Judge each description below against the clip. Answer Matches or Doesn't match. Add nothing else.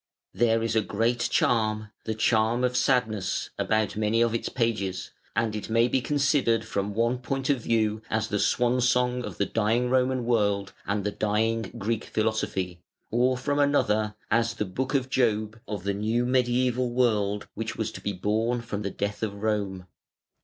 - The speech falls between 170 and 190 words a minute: Matches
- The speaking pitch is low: Matches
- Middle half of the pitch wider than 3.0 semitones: Doesn't match